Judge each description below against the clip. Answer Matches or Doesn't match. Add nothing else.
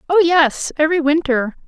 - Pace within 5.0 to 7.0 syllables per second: Matches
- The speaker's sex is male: Doesn't match